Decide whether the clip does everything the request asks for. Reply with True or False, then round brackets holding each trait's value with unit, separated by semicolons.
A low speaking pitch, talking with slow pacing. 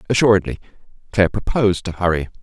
True (95 Hz; 125 wpm)